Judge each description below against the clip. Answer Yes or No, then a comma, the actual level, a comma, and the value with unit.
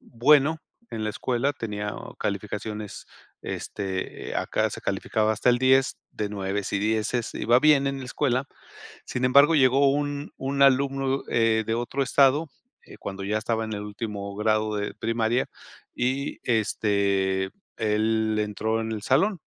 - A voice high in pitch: No, low, 115 Hz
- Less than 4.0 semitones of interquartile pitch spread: No, average, 4.3 semitones